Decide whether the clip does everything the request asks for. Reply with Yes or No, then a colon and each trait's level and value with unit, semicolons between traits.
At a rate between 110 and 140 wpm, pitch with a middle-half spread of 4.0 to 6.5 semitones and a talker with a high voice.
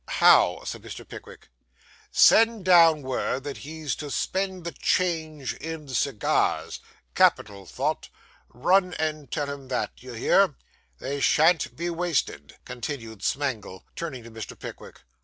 No: slow, 135 wpm; average, 5.0 semitones; medium, 145 Hz